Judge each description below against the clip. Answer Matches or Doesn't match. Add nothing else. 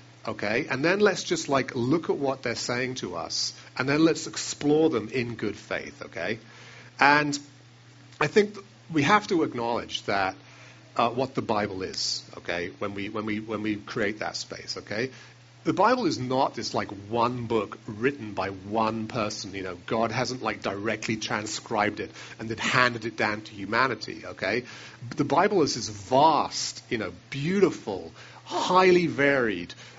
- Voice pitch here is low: Matches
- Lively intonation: Doesn't match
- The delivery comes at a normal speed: Matches